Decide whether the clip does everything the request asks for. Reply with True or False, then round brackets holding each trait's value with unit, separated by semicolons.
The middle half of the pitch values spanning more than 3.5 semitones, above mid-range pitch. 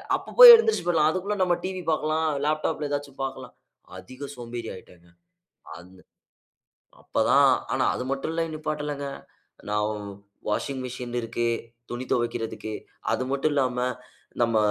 False (4.7 semitones; 135 Hz)